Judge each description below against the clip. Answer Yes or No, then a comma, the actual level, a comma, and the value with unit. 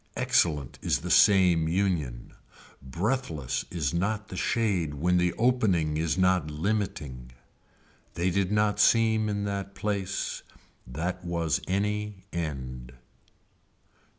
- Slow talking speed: Yes, slow, 115 wpm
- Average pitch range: Yes, average, 4.8 semitones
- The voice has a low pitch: Yes, very low, 90 Hz